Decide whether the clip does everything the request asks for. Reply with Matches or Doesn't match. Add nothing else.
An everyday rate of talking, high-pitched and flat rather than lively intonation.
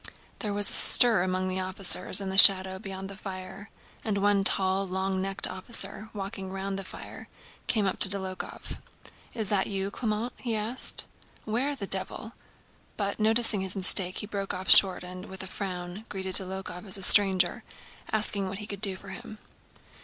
Matches